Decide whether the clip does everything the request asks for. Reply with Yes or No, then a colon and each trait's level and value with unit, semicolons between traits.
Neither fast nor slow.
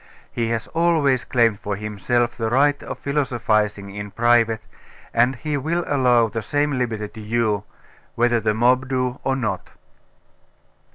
Yes: average, 150 wpm